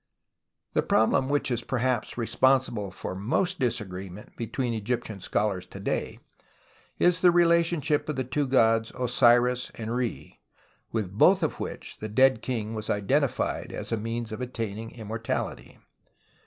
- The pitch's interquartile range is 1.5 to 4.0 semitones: Yes, average, 3.2 semitones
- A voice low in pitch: Yes, low, 120 Hz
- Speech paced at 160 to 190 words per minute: No, average, 145 wpm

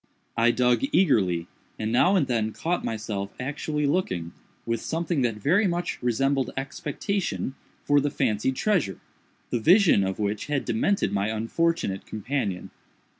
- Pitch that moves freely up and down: Yes, wide, 6.9 semitones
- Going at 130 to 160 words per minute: Yes, average, 140 wpm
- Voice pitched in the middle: No, low, 125 Hz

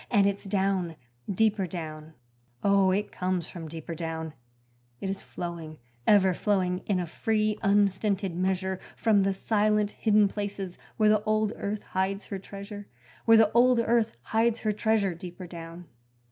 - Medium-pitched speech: No, high, 195 Hz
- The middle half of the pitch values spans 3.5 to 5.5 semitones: No, average, 2.9 semitones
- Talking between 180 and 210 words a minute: No, average, 155 wpm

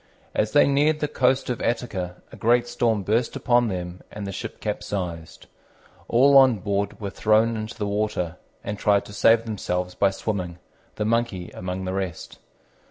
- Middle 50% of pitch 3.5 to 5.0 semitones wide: Yes, average, 3.8 semitones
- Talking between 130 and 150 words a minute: No, average, 170 wpm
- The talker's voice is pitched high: No, low, 105 Hz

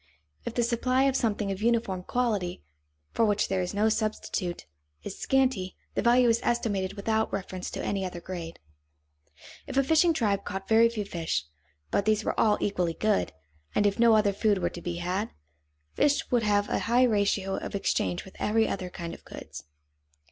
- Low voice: No, high, 205 Hz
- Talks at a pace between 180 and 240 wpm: Yes, average, 185 wpm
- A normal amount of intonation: Yes, average, 3.6 semitones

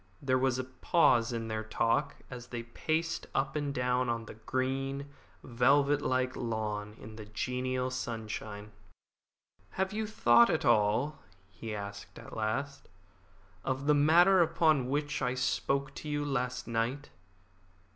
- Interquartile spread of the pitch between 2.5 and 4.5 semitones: Yes, average, 3.6 semitones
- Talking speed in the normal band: Yes, average, 145 wpm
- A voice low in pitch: Yes, low, 130 Hz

